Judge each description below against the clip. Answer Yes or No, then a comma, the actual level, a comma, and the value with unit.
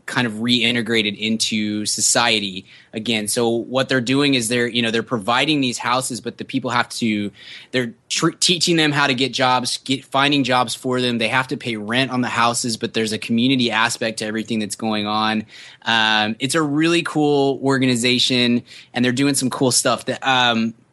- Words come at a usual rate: Yes, average, 195 wpm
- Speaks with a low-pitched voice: Yes, low, 120 Hz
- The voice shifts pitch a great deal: No, average, 2.7 semitones